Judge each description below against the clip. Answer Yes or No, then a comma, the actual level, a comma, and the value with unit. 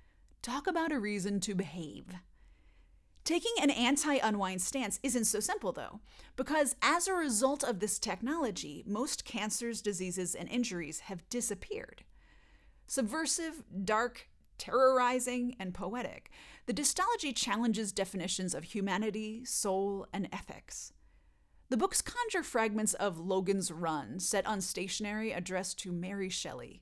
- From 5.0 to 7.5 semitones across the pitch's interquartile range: Yes, wide, 5.4 semitones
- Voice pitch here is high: Yes, high, 215 Hz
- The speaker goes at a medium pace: No, slow, 125 wpm